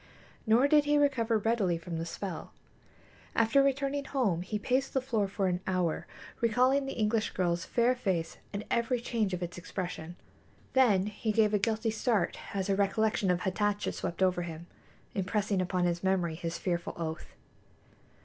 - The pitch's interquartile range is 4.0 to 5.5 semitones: Yes, average, 4.7 semitones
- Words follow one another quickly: No, average, 170 wpm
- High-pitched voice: Yes, high, 205 Hz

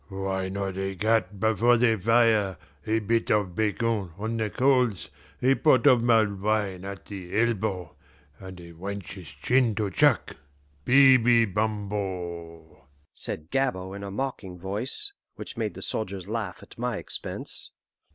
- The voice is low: Yes, low, 105 Hz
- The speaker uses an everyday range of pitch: Yes, average, 3.4 semitones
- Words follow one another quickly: No, average, 145 wpm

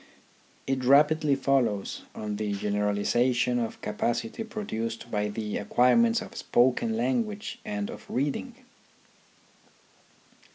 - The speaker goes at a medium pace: No, slow, 110 wpm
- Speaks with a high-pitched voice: No, low, 125 Hz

